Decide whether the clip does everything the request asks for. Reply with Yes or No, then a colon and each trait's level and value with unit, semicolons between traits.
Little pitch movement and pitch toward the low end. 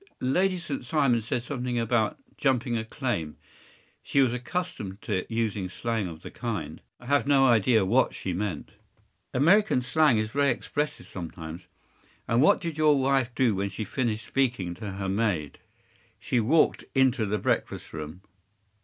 No: average, 5.3 semitones; low, 120 Hz